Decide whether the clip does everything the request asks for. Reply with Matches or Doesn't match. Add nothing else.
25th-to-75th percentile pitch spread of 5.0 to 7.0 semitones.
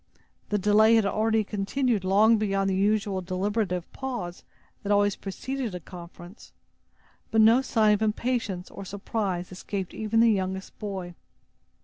Doesn't match